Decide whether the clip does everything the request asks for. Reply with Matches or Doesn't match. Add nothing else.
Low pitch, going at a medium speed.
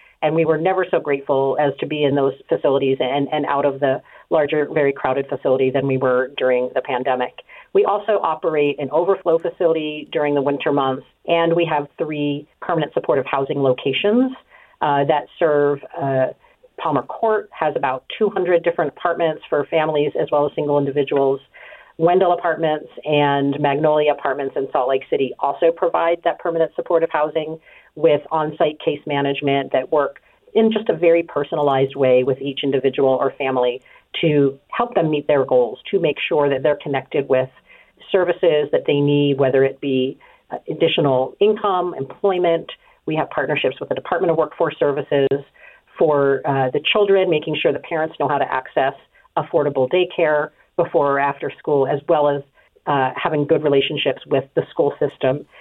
Doesn't match